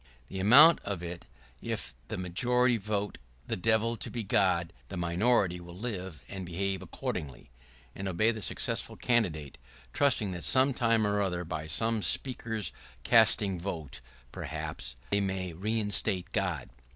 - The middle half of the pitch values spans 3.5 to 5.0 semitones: Yes, average, 4.4 semitones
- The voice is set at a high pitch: No, very low, 95 Hz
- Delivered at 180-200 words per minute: No, average, 155 wpm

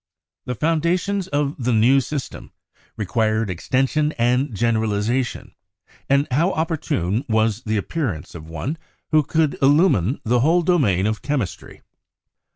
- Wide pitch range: Yes, wide, 5.8 semitones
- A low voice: Yes, low, 125 Hz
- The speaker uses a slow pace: Yes, slow, 125 wpm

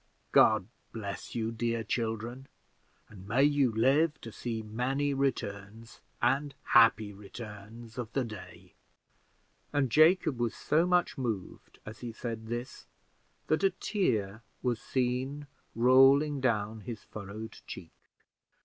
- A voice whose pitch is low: Yes, low, 120 Hz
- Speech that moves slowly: Yes, slow, 125 wpm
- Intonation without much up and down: No, average, 3.8 semitones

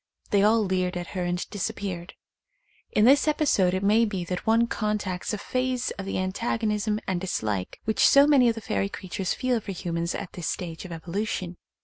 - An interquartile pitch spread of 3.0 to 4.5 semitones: Yes, average, 3.8 semitones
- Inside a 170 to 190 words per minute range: No, average, 200 wpm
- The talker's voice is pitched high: Yes, high, 200 Hz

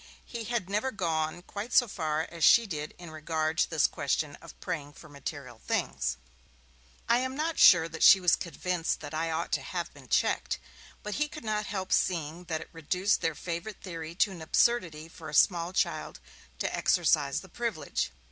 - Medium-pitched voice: Yes, medium, 170 Hz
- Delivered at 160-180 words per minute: No, average, 190 wpm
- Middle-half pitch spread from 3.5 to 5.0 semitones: Yes, average, 4.4 semitones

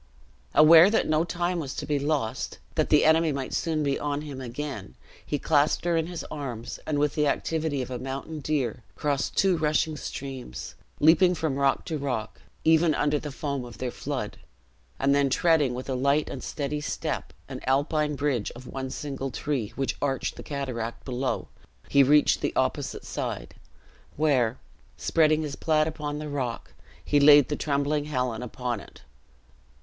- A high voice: No, medium, 145 Hz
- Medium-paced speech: Yes, average, 175 wpm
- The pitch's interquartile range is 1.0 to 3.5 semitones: Yes, narrow, 2.6 semitones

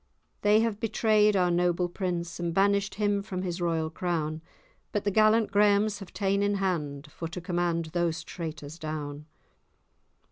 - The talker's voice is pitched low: No, medium, 180 Hz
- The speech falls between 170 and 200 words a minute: No, average, 155 wpm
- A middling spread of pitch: Yes, average, 3.5 semitones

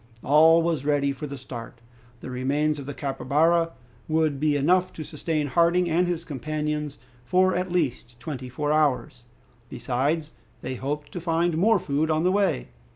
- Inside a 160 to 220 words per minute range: Yes, average, 165 wpm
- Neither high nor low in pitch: Yes, medium, 150 Hz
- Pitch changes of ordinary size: Yes, average, 3.2 semitones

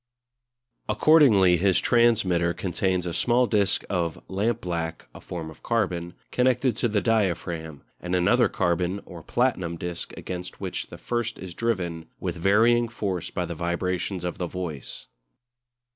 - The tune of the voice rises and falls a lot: No, average, 4.6 semitones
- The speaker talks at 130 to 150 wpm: Yes, average, 145 wpm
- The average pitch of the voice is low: Yes, very low, 90 Hz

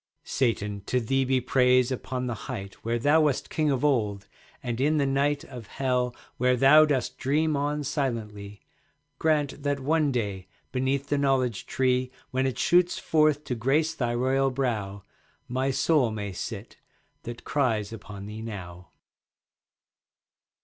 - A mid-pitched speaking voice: No, low, 130 Hz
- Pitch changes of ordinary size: Yes, average, 3.8 semitones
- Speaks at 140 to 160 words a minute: Yes, average, 155 wpm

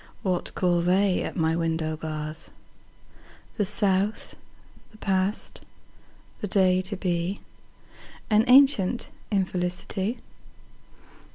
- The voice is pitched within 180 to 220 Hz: Yes, medium, 185 Hz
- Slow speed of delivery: Yes, slow, 85 wpm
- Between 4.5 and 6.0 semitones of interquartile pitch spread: No, average, 2.9 semitones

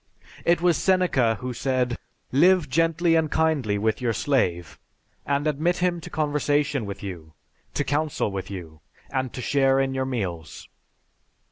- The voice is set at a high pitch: No, low, 135 Hz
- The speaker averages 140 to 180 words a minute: Yes, average, 150 wpm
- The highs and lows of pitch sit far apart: Yes, wide, 6.0 semitones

